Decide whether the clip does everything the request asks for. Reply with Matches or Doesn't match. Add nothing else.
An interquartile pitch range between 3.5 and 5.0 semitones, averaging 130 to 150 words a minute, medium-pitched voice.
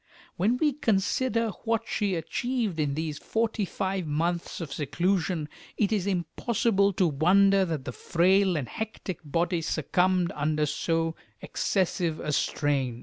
Matches